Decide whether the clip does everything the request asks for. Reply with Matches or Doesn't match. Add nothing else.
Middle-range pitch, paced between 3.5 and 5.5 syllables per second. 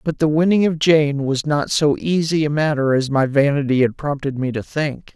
Matches